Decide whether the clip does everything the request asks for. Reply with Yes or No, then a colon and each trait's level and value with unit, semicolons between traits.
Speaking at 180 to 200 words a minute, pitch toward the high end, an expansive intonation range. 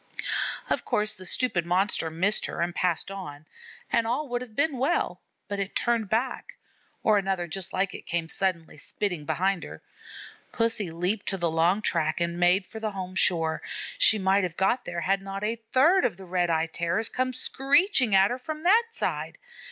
No: average, 190 wpm; high, 195 Hz; average, 5.0 semitones